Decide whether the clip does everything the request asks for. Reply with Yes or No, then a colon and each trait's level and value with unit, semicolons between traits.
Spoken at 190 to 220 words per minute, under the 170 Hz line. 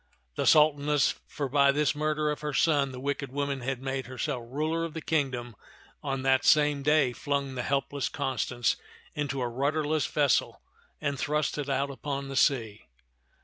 No: average, 175 wpm; medium, 140 Hz